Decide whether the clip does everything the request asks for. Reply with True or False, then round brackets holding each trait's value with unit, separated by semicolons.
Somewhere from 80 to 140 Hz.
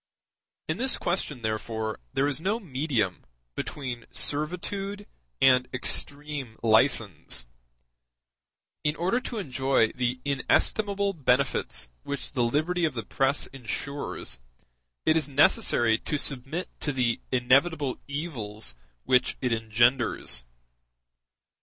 True (135 Hz)